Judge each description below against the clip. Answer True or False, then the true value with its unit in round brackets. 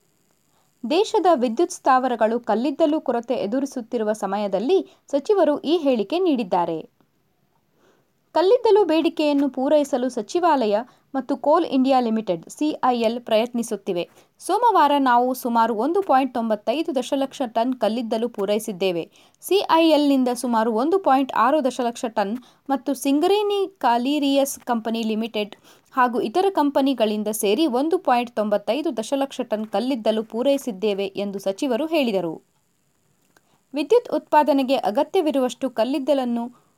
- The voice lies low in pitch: False (260 Hz)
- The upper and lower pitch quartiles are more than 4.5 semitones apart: True (5.2 semitones)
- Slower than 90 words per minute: False (100 wpm)